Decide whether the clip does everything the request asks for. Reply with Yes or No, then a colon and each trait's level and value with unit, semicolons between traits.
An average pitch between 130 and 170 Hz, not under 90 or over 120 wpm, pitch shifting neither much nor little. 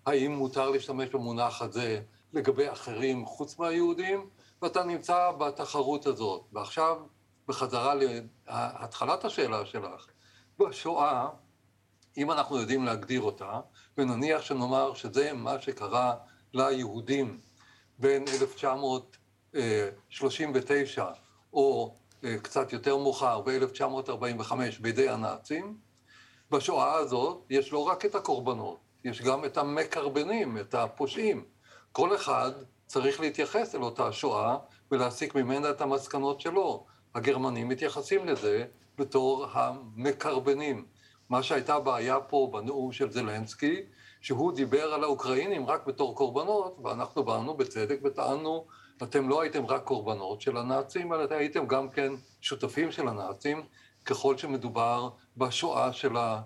Yes: low, 135 Hz; average, 115 wpm; average, 3.2 semitones